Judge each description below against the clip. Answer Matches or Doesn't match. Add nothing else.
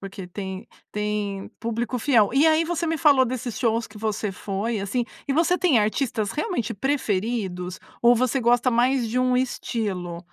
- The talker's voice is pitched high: Matches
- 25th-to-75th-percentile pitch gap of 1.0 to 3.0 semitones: Doesn't match